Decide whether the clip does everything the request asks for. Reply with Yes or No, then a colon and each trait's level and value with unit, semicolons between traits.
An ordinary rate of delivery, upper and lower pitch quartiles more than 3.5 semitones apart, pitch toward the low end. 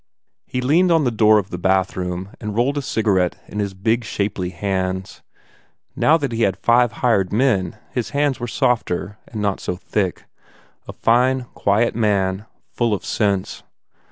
Yes: average, 165 wpm; average, 4.2 semitones; low, 105 Hz